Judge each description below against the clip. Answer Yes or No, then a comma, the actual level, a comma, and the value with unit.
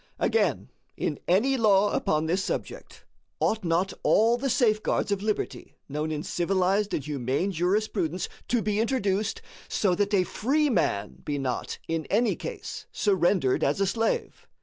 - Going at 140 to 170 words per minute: Yes, average, 150 wpm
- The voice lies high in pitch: Yes, high, 195 Hz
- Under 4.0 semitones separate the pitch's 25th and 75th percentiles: No, average, 4.8 semitones